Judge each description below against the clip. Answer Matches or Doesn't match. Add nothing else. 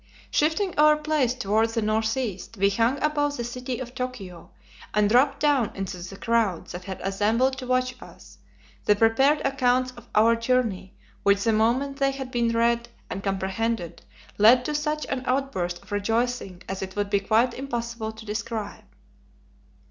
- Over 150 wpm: Matches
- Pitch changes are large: Doesn't match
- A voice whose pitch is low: Doesn't match